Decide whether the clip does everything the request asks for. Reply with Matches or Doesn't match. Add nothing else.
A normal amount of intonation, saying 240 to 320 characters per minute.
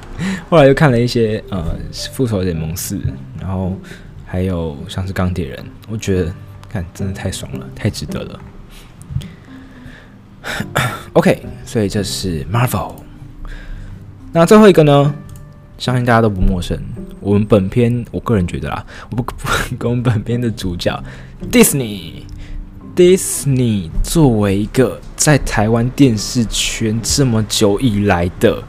Matches